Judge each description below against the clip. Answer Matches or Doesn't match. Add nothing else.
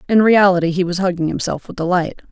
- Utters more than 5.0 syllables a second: Matches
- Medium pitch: Matches